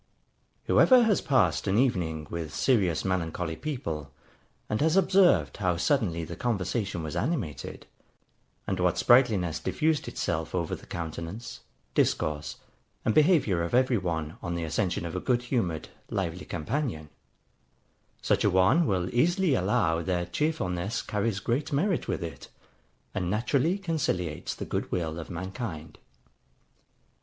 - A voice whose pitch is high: No, very low, 95 Hz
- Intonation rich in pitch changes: Yes, wide, 7.6 semitones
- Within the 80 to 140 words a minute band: Yes, slow, 135 wpm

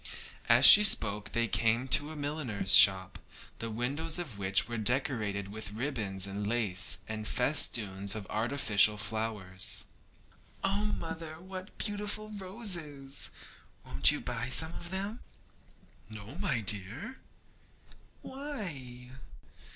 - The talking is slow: Yes, slow, 120 wpm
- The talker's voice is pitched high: No, low, 120 Hz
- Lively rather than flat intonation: Yes, wide, 7.9 semitones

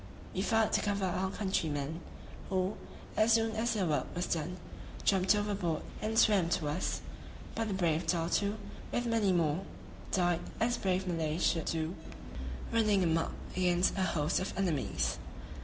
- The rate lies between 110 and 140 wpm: No, average, 155 wpm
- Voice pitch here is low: No, medium, 185 Hz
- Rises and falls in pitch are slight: No, average, 3.8 semitones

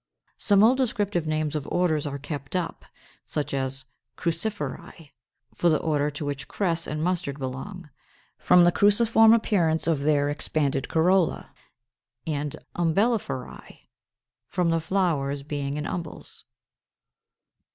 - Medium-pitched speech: Yes, medium, 160 Hz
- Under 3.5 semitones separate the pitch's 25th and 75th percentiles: No, average, 4.1 semitones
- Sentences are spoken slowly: Yes, slow, 125 wpm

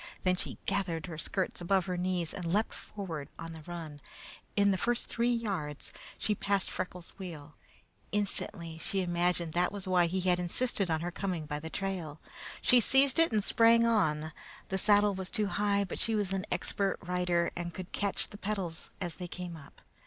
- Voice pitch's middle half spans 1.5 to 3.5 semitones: Yes, average, 3.0 semitones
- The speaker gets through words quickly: No, average, 190 wpm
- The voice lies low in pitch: No, medium, 185 Hz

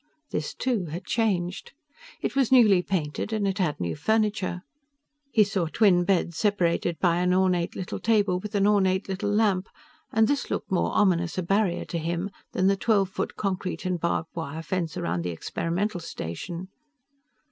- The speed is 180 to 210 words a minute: No, average, 170 wpm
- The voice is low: No, medium, 185 Hz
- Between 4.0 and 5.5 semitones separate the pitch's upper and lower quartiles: No, average, 3.2 semitones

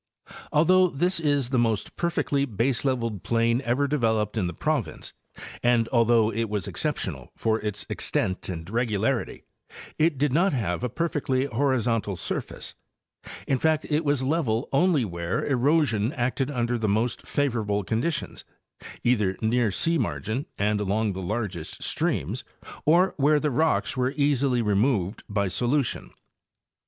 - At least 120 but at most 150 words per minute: Yes, average, 140 wpm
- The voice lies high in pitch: No, low, 120 Hz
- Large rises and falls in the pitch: No, average, 5.0 semitones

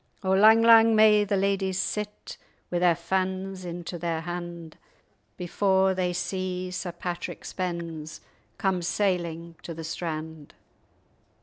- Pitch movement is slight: Yes, narrow, 2.1 semitones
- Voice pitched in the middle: Yes, medium, 180 Hz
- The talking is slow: Yes, slow, 125 wpm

